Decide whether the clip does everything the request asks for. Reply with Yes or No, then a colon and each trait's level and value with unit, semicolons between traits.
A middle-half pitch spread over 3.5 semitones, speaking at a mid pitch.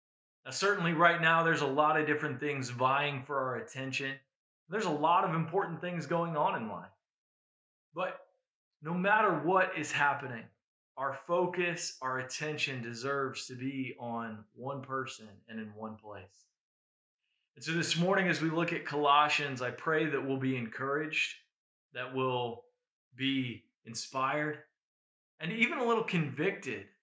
Yes: average, 4.5 semitones; medium, 145 Hz